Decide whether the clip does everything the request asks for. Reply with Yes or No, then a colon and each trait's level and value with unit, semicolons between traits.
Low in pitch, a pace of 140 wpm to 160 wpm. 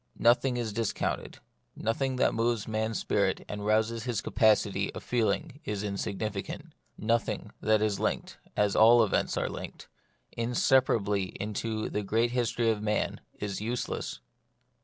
Yes: low, 110 Hz; average, 145 wpm